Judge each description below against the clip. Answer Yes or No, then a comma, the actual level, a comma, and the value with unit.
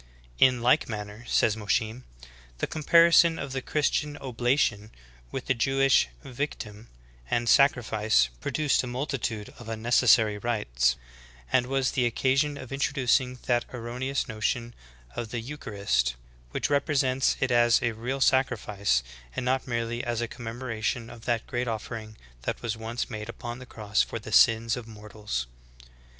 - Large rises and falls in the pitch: No, average, 3.0 semitones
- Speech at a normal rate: Yes, average, 150 wpm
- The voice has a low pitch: Yes, low, 120 Hz